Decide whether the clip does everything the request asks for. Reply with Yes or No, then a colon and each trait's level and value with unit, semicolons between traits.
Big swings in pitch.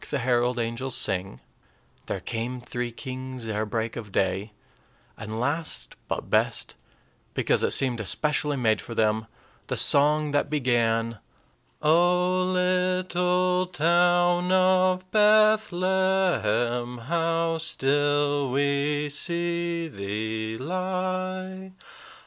Yes: wide, 7.2 semitones